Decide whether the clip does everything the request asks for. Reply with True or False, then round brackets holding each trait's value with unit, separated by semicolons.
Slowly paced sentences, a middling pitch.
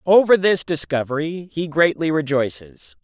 True (120 wpm; 155 Hz)